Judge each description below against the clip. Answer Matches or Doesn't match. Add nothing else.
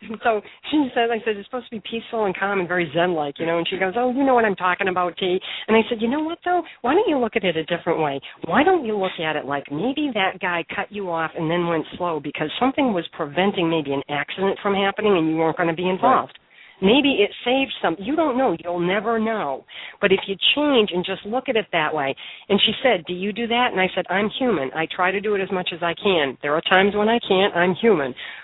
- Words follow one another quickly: Matches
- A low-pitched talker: Doesn't match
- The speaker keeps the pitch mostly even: Doesn't match